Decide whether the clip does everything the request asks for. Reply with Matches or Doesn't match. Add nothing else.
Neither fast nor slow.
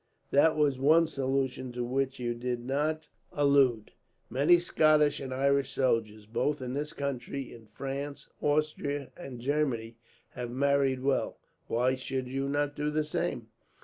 Matches